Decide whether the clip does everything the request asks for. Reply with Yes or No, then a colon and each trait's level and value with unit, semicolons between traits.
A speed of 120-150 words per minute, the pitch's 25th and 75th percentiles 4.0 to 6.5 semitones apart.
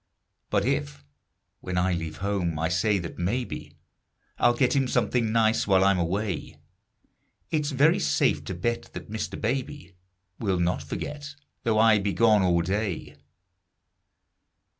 Yes: average, 140 wpm; average, 4.8 semitones